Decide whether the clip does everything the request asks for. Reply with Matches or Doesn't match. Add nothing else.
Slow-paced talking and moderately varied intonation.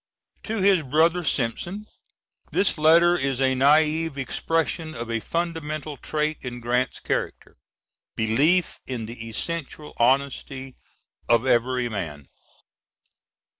Matches